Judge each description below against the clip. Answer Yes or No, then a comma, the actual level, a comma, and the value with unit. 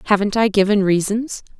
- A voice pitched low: No, high, 205 Hz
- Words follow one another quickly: No, average, 150 wpm